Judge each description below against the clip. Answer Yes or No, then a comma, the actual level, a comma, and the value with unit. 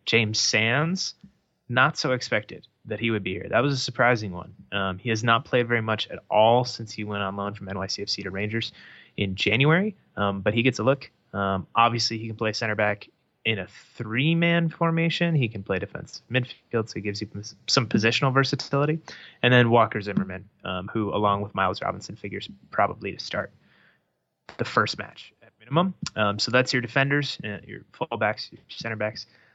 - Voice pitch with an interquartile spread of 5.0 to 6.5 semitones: No, average, 4.0 semitones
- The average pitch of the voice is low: Yes, low, 115 Hz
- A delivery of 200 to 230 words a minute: No, average, 190 wpm